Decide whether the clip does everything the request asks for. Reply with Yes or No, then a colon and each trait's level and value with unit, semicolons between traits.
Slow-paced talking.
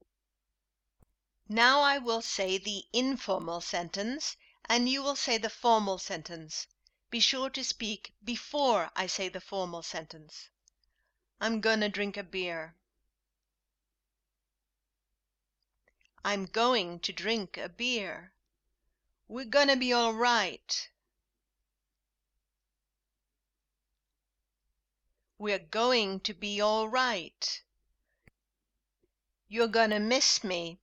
Yes: slow, 95 wpm